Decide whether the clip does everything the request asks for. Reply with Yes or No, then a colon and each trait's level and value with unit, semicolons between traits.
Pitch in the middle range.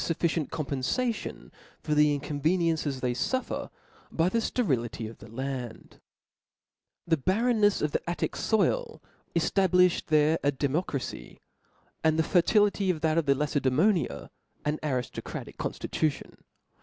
Yes: medium, 155 Hz